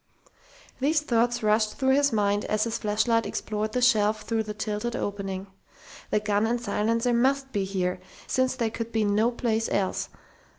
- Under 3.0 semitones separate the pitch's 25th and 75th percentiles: Yes, narrow, 2.4 semitones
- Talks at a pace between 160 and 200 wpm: Yes, average, 170 wpm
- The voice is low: No, high, 220 Hz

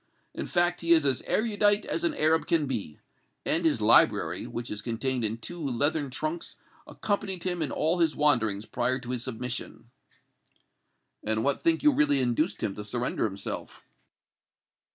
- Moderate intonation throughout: No, wide, 6.1 semitones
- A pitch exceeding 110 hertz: Yes, medium, 140 Hz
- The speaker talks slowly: No, average, 165 wpm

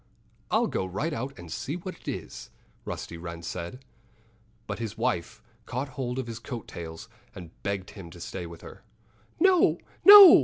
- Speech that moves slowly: No, average, 175 wpm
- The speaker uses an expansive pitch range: Yes, wide, 7.7 semitones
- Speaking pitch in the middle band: No, low, 115 Hz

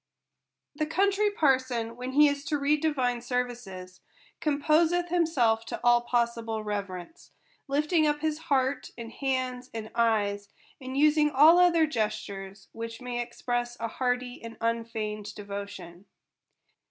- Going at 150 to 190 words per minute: No, average, 140 wpm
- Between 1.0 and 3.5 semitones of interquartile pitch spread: No, average, 4.8 semitones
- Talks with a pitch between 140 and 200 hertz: No, high, 245 Hz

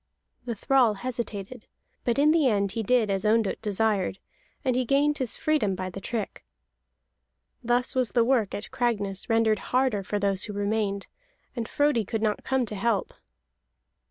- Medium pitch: No, high, 225 Hz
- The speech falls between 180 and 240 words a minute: No, average, 165 wpm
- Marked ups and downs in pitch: No, average, 3.8 semitones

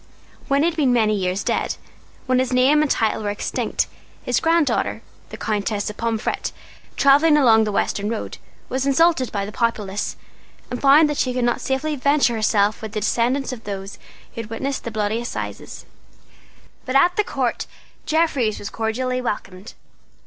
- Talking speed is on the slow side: No, average, 170 wpm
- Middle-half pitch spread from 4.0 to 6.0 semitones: Yes, average, 4.5 semitones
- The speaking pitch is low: No, high, 240 Hz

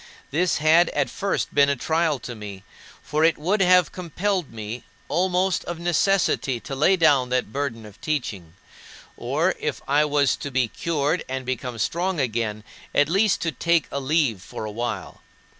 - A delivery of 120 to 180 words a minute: Yes, average, 175 wpm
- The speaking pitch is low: No, medium, 145 Hz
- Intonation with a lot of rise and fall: Yes, wide, 5.7 semitones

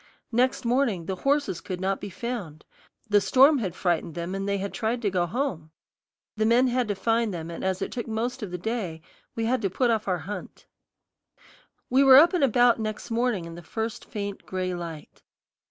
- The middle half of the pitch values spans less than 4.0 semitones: No, average, 4.9 semitones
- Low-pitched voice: No, high, 215 Hz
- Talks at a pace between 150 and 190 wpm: No, fast, 205 wpm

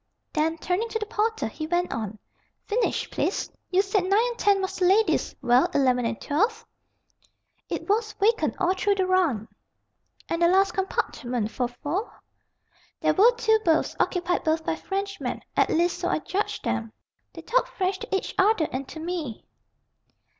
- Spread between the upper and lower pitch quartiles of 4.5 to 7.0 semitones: Yes, average, 4.9 semitones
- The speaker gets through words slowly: No, average, 170 wpm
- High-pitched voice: Yes, very high, 370 Hz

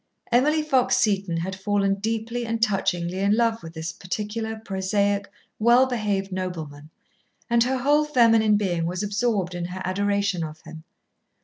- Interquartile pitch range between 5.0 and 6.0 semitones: No, average, 3.7 semitones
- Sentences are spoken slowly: No, average, 150 wpm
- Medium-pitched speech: No, high, 200 Hz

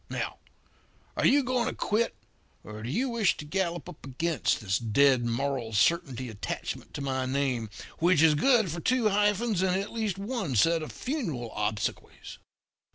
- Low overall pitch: No, medium, 165 Hz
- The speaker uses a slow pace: No, average, 170 wpm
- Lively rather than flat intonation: Yes, wide, 8.3 semitones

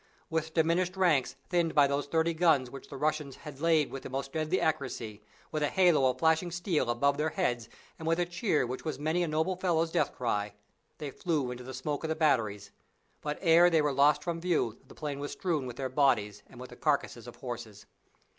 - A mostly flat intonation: No, average, 4.0 semitones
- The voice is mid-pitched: Yes, medium, 150 Hz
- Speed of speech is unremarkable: No, fast, 220 wpm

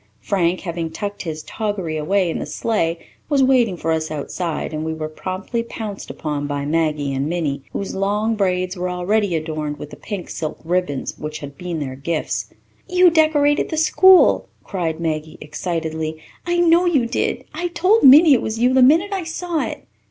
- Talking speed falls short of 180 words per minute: No, average, 185 wpm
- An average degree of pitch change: No, wide, 8.0 semitones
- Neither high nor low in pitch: Yes, medium, 180 Hz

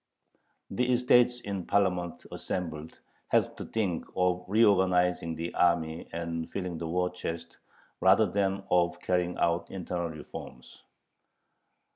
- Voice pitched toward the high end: No, very low, 90 Hz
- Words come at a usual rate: No, slow, 120 wpm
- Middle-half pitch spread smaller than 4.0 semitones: Yes, narrow, 2.4 semitones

